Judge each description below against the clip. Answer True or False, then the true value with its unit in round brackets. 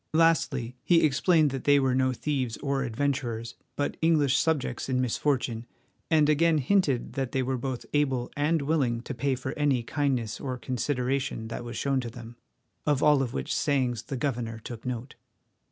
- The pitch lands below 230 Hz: True (135 Hz)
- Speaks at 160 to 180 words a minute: True (175 wpm)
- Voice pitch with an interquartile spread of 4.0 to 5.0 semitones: False (3.1 semitones)